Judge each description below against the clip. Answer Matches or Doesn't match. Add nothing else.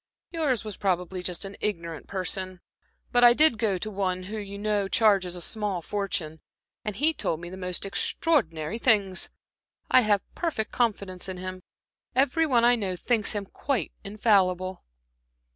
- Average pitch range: Matches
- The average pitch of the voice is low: Doesn't match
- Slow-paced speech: Doesn't match